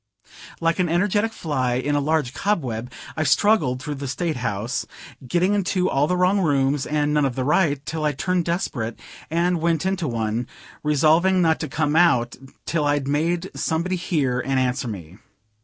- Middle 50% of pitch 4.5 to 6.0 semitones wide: Yes, average, 4.8 semitones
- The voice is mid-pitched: Yes, medium, 150 Hz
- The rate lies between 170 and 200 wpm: Yes, average, 180 wpm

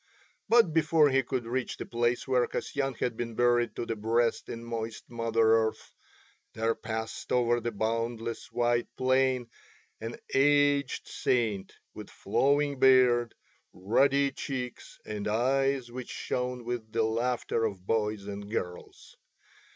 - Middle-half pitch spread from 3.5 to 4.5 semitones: No, narrow, 2.5 semitones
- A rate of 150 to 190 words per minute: No, slow, 135 wpm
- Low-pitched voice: Yes, low, 120 Hz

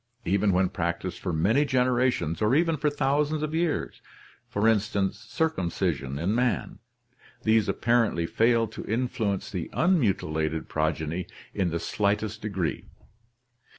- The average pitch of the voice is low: Yes, low, 105 Hz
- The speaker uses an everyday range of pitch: No, wide, 6.7 semitones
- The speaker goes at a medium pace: No, slow, 120 wpm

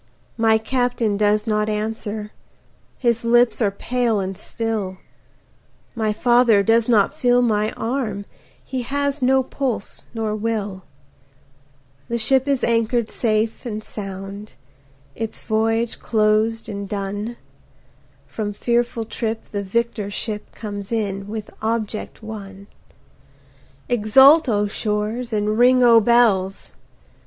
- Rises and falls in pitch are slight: Yes, narrow, 2.3 semitones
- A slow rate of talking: Yes, slow, 120 wpm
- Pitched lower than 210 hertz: No, high, 220 Hz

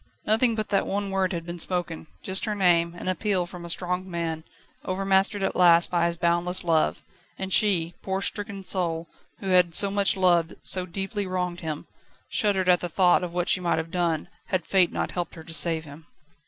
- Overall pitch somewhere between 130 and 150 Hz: No, medium, 180 Hz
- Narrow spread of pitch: Yes, narrow, 2.2 semitones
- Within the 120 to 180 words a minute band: No, fast, 205 wpm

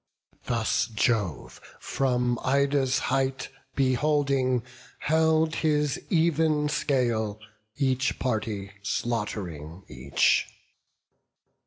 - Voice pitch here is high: No, low, 130 Hz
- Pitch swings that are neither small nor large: Yes, average, 4.8 semitones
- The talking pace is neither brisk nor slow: No, slow, 70 wpm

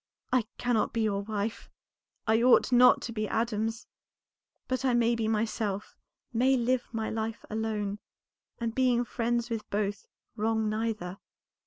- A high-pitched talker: Yes, high, 225 Hz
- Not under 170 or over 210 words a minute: No, average, 145 wpm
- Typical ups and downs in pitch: No, narrow, 1.9 semitones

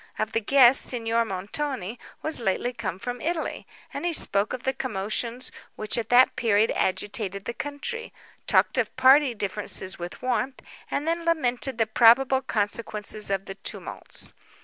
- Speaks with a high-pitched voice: Yes, high, 235 Hz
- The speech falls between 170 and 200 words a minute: No, average, 155 wpm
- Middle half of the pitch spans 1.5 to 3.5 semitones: No, average, 4.2 semitones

